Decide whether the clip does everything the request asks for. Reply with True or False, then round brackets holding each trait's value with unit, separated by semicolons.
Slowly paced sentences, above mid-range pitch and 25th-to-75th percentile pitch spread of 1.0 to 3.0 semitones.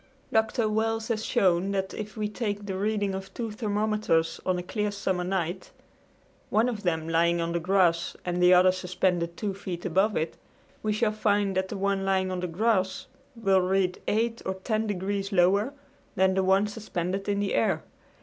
False (190 wpm; 195 Hz; 2.6 semitones)